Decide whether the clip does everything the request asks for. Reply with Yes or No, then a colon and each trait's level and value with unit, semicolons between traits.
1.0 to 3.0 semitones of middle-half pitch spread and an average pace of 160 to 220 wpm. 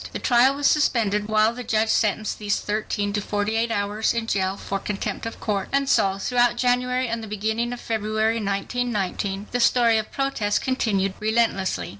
Yes: narrow, 2.6 semitones; average, 180 wpm